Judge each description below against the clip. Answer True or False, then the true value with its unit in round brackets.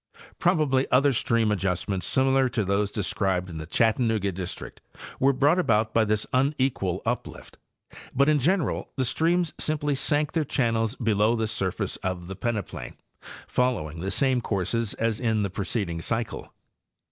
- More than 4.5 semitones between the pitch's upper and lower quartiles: True (5.2 semitones)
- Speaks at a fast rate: False (160 wpm)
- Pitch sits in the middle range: False (115 Hz)